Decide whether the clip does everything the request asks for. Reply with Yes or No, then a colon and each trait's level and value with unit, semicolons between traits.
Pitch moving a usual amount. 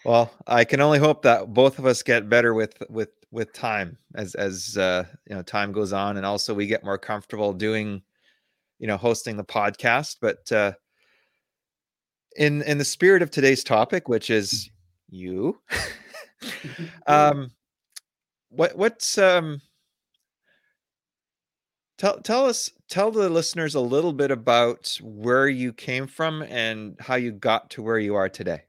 No: wide, 5.9 semitones